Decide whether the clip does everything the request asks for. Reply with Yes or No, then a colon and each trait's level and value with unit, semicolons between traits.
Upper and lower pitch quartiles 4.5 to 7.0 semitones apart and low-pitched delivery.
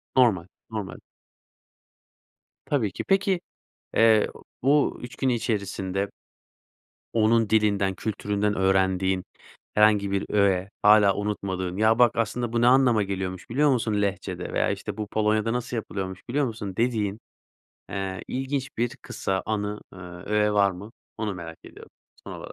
No: average, 3.0 semitones; low, 105 Hz